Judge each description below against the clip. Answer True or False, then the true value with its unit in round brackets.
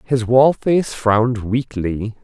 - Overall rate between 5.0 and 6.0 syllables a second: False (3.8 syllables/s)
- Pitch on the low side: True (120 Hz)